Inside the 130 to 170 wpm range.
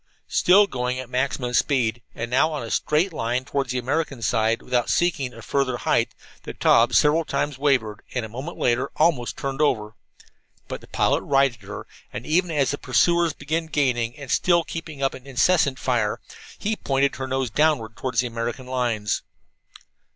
No: average, 180 wpm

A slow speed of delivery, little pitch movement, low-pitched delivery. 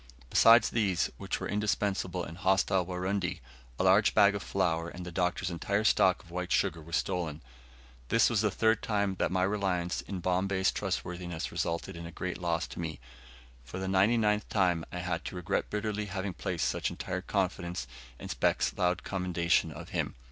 No: average, 185 wpm; narrow, 2.3 semitones; very low, 90 Hz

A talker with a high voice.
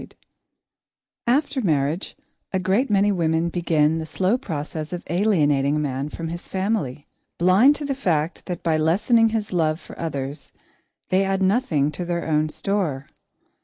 No: medium, 170 Hz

